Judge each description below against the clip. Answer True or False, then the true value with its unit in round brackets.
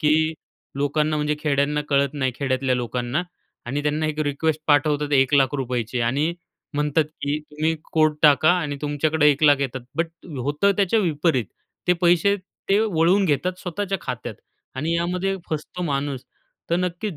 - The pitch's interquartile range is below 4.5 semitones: True (3.1 semitones)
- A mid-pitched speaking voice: True (150 Hz)